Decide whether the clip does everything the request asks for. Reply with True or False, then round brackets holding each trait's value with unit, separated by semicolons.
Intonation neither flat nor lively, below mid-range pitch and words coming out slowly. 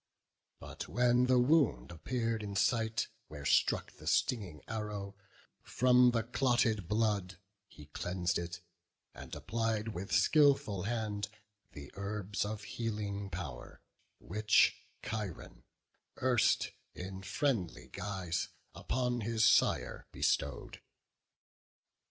True (3.5 semitones; 105 Hz; 105 wpm)